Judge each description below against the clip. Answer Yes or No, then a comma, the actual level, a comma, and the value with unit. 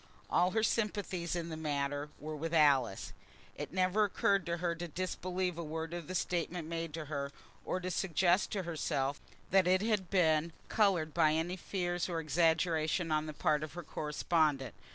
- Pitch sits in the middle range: Yes, medium, 170 Hz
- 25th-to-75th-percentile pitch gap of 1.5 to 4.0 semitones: Yes, average, 2.8 semitones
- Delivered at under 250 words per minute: Yes, average, 180 wpm